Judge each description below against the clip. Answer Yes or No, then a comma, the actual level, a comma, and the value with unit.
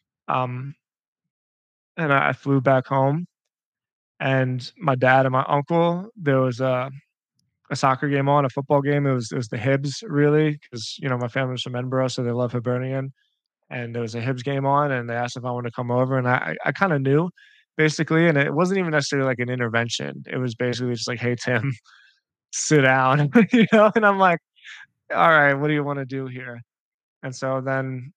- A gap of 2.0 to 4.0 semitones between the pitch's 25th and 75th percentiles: Yes, narrow, 2.6 semitones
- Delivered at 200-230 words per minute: Yes, fast, 205 wpm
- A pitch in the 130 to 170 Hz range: Yes, low, 135 Hz